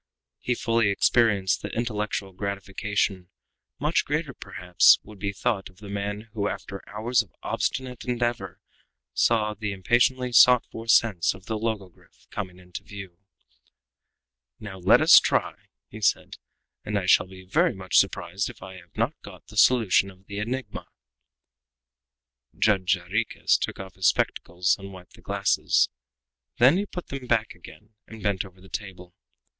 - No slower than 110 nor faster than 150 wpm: No, average, 160 wpm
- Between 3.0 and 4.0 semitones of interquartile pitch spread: Yes, average, 3.4 semitones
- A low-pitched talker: Yes, low, 100 Hz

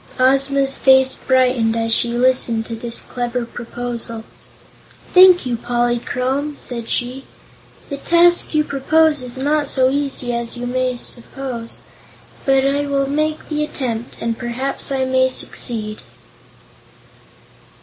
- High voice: Yes, very high, 255 Hz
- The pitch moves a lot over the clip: No, narrow, 2.6 semitones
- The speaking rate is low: Yes, slow, 125 wpm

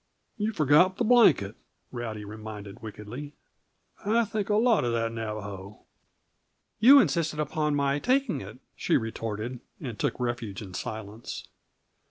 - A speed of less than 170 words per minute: Yes, slow, 135 wpm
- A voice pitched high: No, low, 120 Hz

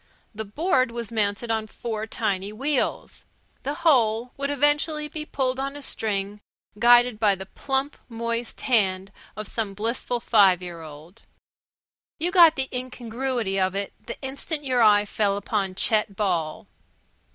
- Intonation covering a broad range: No, average, 4.7 semitones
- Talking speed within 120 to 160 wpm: Yes, average, 150 wpm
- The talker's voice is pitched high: Yes, high, 225 Hz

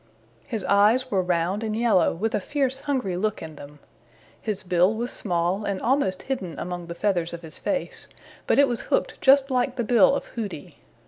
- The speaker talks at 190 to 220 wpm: Yes, average, 195 wpm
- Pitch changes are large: Yes, wide, 5.9 semitones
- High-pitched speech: Yes, high, 210 Hz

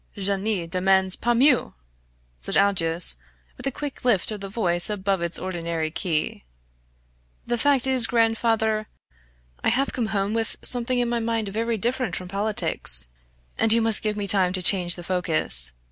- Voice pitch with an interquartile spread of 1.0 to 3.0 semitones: No, average, 4.1 semitones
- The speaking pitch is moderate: No, high, 205 Hz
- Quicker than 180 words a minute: No, average, 170 wpm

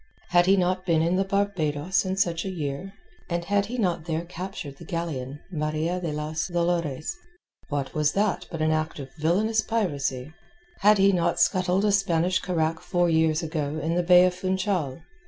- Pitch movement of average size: Yes, average, 3.1 semitones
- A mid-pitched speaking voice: Yes, medium, 170 Hz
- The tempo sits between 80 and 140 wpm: No, average, 185 wpm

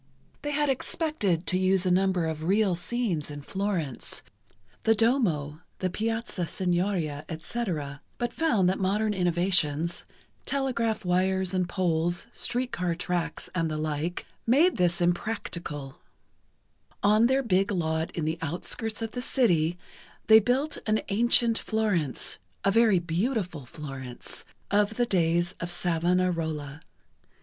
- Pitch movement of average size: Yes, average, 5.0 semitones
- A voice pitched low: No, medium, 185 Hz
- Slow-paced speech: Yes, slow, 125 wpm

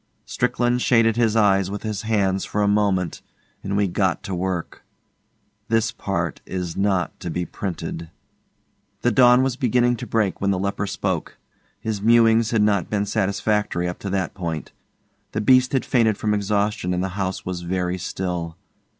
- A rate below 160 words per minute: No, average, 170 wpm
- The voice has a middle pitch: No, low, 100 Hz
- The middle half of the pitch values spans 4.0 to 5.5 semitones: No, average, 3.3 semitones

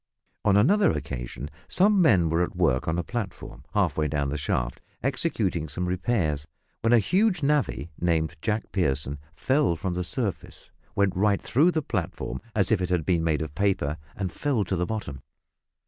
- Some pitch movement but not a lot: No, wide, 6.6 semitones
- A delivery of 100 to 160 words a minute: No, average, 180 wpm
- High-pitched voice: No, very low, 90 Hz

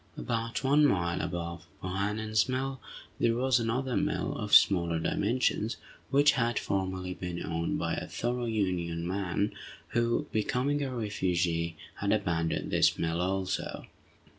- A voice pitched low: Yes, low, 100 Hz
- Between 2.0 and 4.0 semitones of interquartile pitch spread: No, average, 5.3 semitones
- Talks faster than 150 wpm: No, slow, 135 wpm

